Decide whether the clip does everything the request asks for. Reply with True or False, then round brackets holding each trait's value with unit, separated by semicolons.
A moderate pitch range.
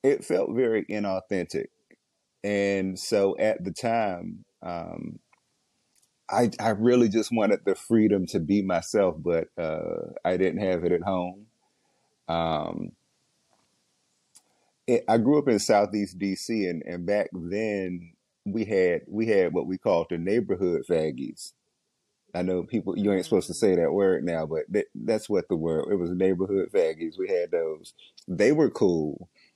True (3.8 semitones)